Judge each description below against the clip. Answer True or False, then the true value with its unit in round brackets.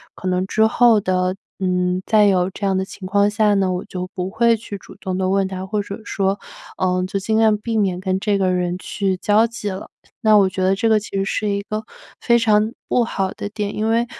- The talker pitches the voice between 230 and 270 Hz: False (200 Hz)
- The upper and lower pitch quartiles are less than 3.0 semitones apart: True (2.4 semitones)